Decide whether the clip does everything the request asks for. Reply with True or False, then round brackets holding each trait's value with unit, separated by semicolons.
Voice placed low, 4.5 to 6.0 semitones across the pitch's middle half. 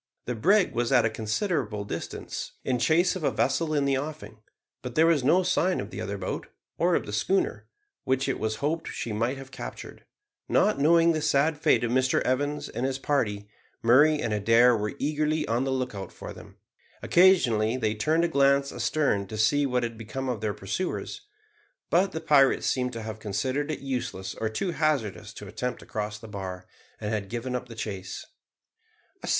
True (130 Hz; 5.6 semitones)